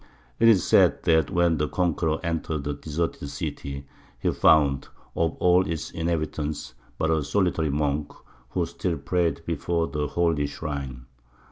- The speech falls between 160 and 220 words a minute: No, average, 145 wpm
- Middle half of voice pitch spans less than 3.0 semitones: Yes, narrow, 2.6 semitones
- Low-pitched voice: Yes, very low, 80 Hz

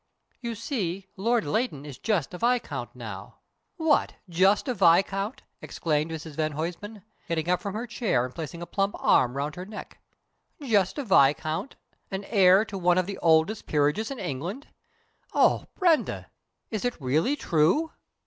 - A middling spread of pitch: No, wide, 5.7 semitones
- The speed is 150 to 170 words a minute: Yes, average, 165 wpm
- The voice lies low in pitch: No, high, 190 Hz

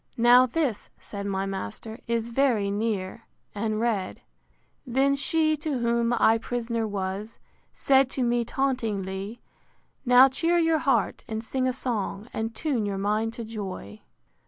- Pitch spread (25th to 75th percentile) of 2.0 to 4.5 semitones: Yes, average, 3.8 semitones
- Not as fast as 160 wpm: Yes, average, 150 wpm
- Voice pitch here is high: Yes, high, 230 Hz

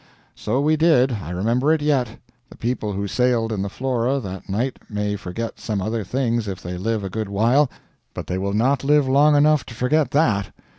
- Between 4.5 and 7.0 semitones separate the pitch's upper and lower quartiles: Yes, average, 4.9 semitones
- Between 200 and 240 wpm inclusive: Yes, fast, 205 wpm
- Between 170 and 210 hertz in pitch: No, low, 115 Hz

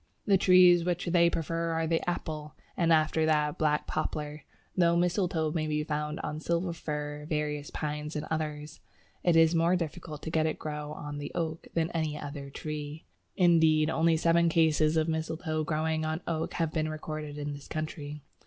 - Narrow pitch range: Yes, narrow, 1.7 semitones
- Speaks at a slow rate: No, average, 185 wpm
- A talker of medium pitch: Yes, medium, 155 Hz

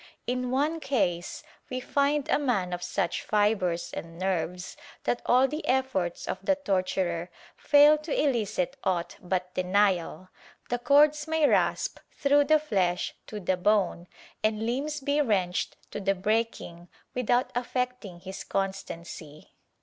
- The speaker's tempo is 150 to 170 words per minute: No, average, 140 wpm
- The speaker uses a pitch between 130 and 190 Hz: No, high, 215 Hz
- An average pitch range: No, wide, 6.8 semitones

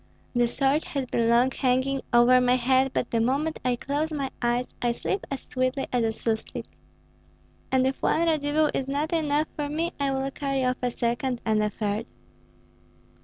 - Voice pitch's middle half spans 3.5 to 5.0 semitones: No, average, 3.0 semitones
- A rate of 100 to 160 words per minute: No, average, 185 wpm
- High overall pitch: Yes, very high, 260 Hz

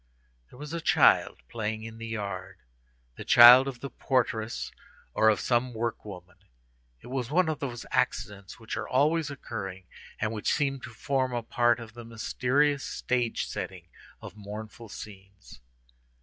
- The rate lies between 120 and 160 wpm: Yes, average, 155 wpm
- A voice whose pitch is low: Yes, low, 115 Hz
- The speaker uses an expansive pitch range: No, average, 3.6 semitones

